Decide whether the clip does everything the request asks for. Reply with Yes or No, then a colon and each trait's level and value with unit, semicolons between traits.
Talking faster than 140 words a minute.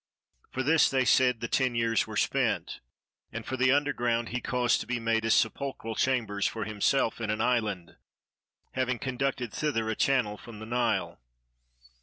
Yes: average, 170 wpm